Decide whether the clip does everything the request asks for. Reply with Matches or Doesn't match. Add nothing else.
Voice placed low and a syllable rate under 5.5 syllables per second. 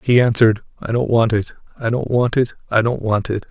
Doesn't match